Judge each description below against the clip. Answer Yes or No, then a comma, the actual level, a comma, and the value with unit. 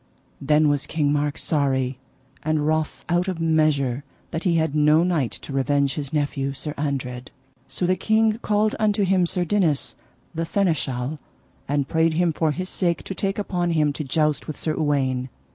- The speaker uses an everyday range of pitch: Yes, average, 3.6 semitones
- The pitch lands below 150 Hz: No, medium, 155 Hz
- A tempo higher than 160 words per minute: Yes, average, 180 wpm